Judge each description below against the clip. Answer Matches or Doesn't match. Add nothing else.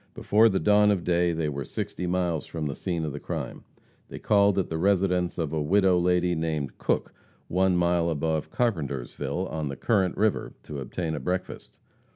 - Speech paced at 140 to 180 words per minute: Doesn't match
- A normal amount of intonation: Matches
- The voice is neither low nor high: Doesn't match